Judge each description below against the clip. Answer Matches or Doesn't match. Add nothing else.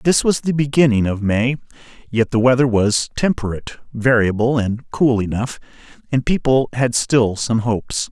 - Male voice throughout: Matches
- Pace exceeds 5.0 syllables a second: Doesn't match